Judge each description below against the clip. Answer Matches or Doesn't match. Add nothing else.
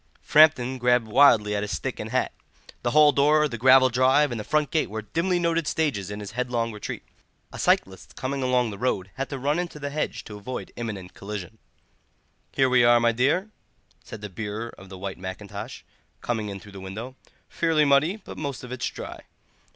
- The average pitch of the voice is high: Doesn't match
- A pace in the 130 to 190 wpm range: Doesn't match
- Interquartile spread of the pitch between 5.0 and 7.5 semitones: Matches